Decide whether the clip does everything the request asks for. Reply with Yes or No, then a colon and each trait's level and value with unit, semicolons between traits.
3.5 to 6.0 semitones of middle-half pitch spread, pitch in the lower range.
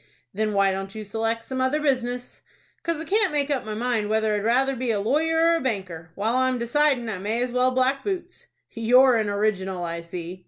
No: average, 4.3 semitones; high, 235 Hz